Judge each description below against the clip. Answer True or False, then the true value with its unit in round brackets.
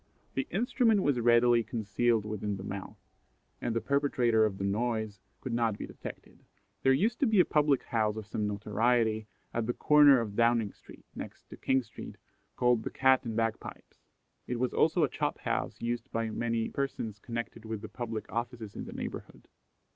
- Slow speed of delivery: False (185 wpm)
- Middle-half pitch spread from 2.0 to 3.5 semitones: True (3.2 semitones)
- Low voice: True (115 Hz)